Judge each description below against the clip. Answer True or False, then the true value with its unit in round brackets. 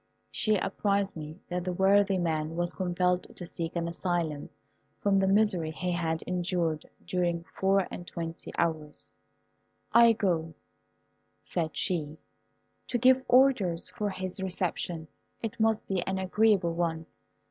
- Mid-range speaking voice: True (180 Hz)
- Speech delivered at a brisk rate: False (135 wpm)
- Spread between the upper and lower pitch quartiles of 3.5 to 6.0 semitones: False (2.8 semitones)